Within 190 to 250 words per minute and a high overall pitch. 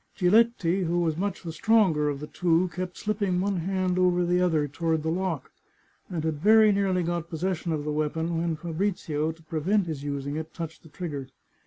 No: average, 200 wpm; medium, 170 Hz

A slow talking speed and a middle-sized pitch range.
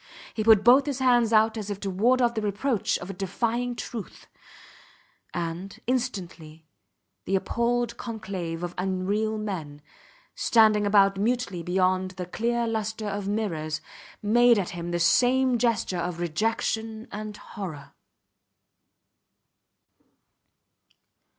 Yes: slow, 125 wpm; average, 4.1 semitones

